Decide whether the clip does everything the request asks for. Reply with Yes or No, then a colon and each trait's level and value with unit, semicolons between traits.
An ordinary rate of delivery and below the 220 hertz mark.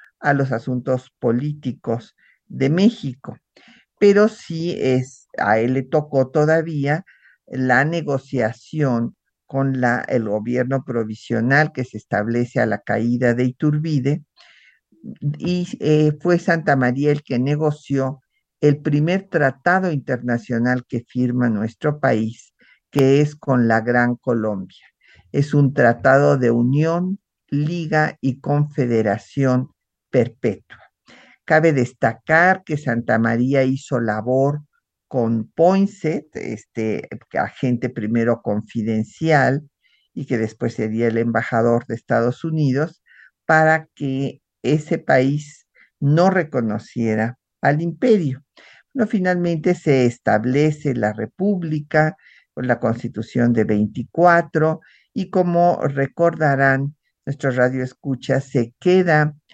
No: slow, 110 wpm; low, 135 Hz